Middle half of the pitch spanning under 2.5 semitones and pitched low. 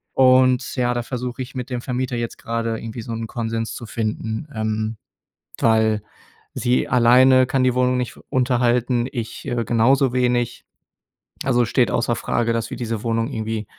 Yes: narrow, 1.8 semitones; low, 120 Hz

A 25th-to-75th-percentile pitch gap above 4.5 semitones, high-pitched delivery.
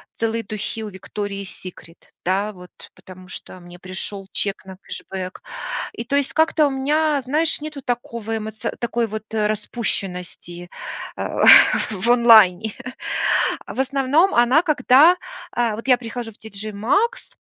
Yes: average, 5.2 semitones; high, 225 Hz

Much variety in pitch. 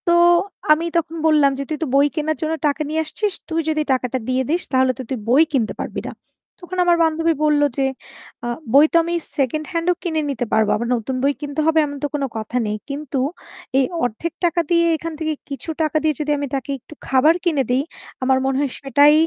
No: average, 3.2 semitones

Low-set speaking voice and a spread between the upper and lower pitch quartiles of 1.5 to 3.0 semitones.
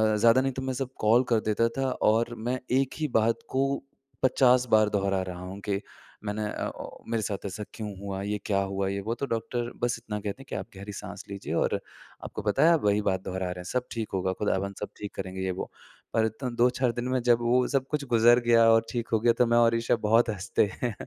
No: low, 115 Hz; average, 3.5 semitones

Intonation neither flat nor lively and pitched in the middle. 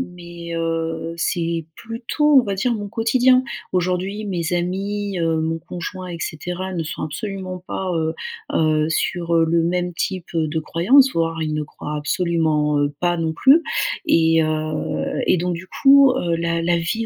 Yes: average, 3.0 semitones; medium, 170 Hz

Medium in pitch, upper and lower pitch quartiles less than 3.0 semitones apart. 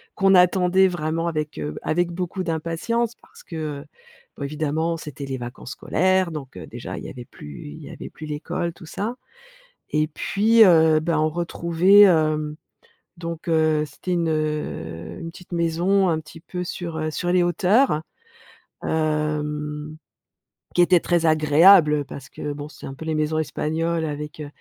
Yes: medium, 160 Hz; narrow, 2.6 semitones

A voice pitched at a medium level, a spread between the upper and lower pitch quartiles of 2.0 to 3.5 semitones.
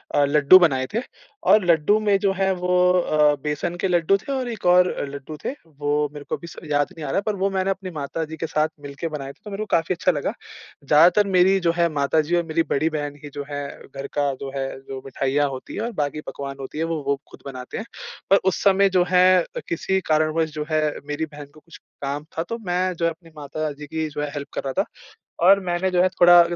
No: medium, 160 Hz; average, 4.1 semitones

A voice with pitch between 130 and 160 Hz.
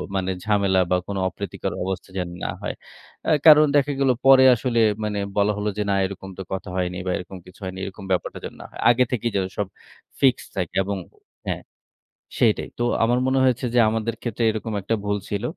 No: low, 105 Hz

